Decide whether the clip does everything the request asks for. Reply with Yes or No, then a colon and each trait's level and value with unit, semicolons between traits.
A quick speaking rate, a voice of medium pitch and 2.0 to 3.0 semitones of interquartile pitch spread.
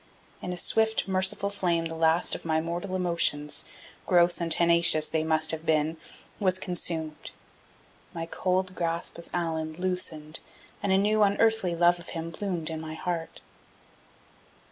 No: average, 150 wpm; medium, 170 Hz; narrow, 2.4 semitones